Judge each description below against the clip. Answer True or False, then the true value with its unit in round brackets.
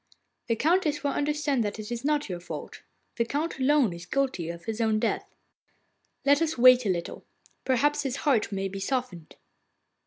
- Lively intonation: True (5.7 semitones)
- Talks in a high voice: True (255 Hz)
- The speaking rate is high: False (180 wpm)